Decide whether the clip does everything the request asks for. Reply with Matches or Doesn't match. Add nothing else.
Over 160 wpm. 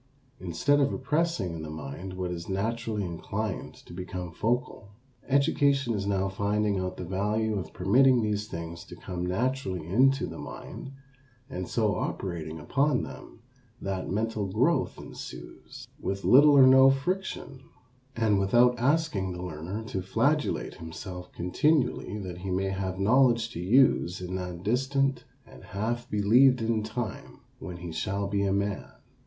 Doesn't match